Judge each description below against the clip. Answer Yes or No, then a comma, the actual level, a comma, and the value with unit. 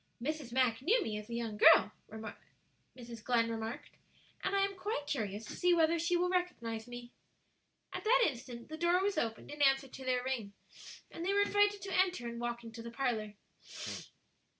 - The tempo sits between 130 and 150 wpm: No, average, 190 wpm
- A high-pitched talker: Yes, very high, 260 Hz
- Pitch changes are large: Yes, wide, 7.3 semitones